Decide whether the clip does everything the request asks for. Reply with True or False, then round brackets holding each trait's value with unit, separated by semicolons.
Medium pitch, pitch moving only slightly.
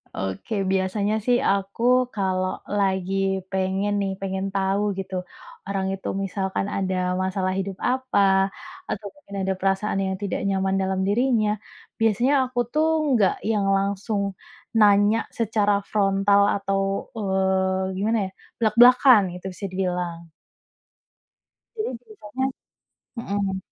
False (195 Hz; 1.9 semitones)